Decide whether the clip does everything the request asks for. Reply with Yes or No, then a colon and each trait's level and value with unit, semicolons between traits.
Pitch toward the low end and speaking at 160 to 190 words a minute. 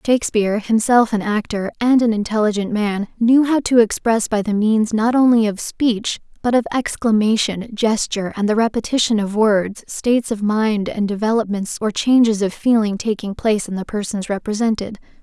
No: high, 220 Hz; average, 170 wpm